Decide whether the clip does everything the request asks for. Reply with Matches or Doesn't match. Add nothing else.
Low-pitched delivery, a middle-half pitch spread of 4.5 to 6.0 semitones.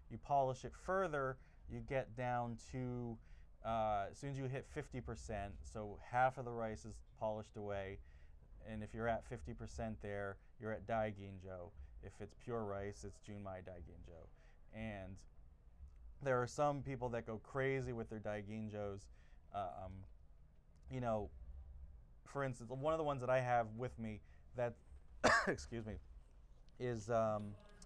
Matches